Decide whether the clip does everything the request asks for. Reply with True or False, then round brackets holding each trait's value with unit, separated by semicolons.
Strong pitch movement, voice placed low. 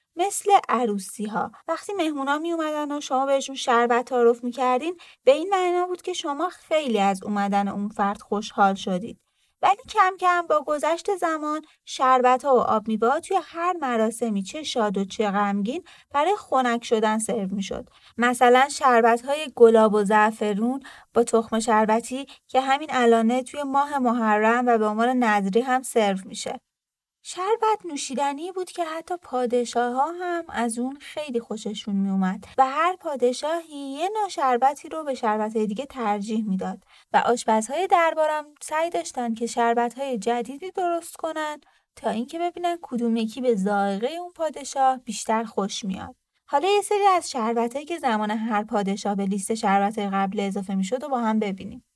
False (5.9 semitones; 250 Hz)